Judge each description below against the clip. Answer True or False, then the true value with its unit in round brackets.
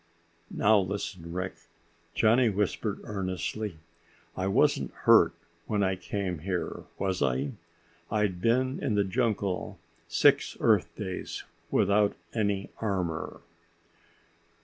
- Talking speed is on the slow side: True (105 wpm)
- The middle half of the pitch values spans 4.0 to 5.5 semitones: False (2.5 semitones)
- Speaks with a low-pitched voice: True (100 Hz)